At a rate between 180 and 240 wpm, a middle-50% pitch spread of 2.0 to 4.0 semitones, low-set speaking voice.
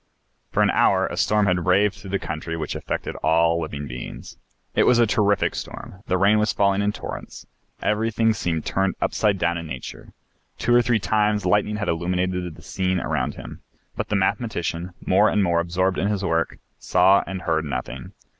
Yes: average, 190 wpm; average, 3.6 semitones; very low, 95 Hz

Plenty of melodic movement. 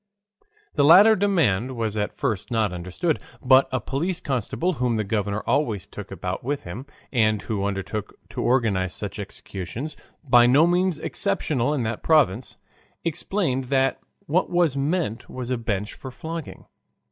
Yes: wide, 6.5 semitones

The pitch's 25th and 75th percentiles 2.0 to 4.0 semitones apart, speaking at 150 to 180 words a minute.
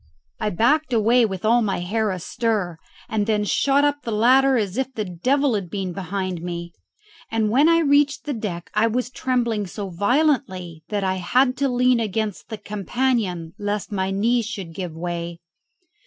No: average, 5.0 semitones; average, 175 wpm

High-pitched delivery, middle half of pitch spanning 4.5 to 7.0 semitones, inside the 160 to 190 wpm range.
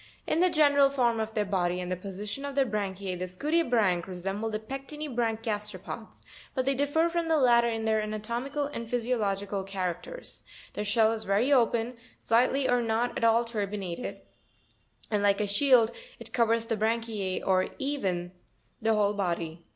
No: high, 225 Hz; average, 4.1 semitones; average, 170 wpm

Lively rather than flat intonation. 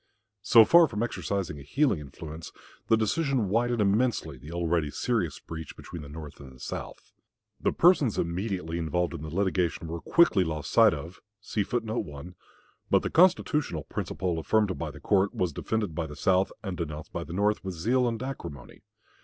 Yes: wide, 5.7 semitones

